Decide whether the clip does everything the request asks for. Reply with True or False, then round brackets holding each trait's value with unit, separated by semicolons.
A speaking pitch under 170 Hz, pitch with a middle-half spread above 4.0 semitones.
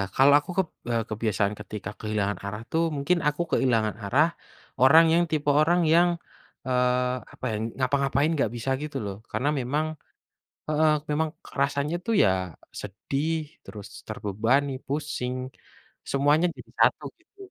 True (140 Hz; 5.2 semitones)